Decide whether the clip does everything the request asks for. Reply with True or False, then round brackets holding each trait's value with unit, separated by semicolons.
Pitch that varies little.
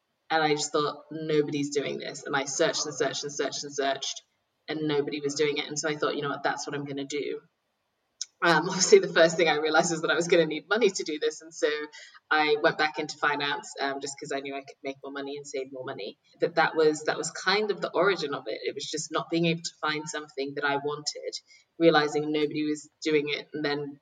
True (1.6 semitones)